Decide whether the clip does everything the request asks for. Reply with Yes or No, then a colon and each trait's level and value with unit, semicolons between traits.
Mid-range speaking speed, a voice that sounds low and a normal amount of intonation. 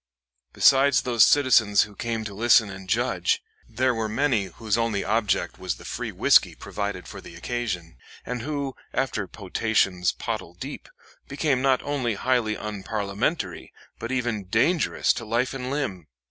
Yes: average, 150 wpm; low, 115 Hz; average, 4.2 semitones